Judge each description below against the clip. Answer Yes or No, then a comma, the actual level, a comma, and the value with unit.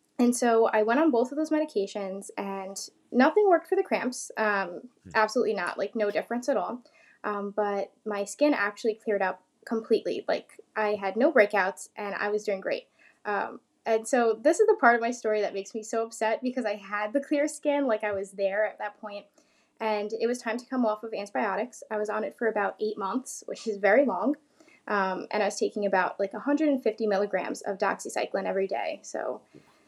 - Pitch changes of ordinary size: Yes, average, 3.8 semitones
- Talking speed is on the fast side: Yes, fast, 210 wpm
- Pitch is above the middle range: Yes, high, 220 Hz